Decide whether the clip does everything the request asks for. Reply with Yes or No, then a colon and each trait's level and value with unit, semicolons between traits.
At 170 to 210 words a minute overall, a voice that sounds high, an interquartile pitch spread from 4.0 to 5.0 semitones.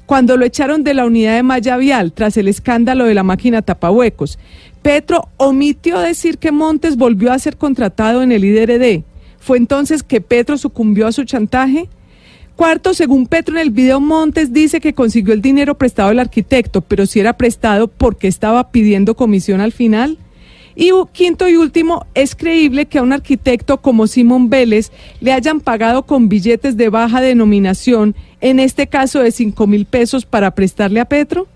Yes: average, 180 wpm; very high, 255 Hz; average, 4.3 semitones